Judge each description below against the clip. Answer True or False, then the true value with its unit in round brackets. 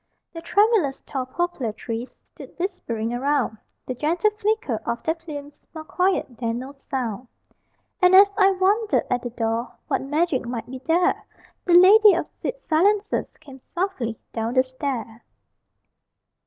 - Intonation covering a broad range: True (7.0 semitones)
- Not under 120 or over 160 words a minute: True (150 wpm)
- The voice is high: True (290 Hz)